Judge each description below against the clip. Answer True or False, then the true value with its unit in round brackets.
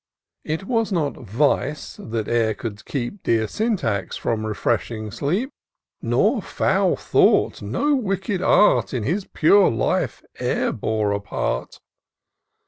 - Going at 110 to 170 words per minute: True (135 wpm)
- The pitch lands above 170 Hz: False (135 Hz)